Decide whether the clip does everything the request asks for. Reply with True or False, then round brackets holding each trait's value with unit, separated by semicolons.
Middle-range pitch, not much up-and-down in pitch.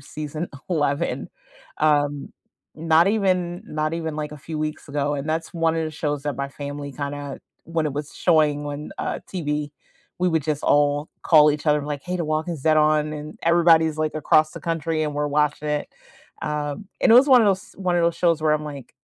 True (155 Hz; 2.0 semitones)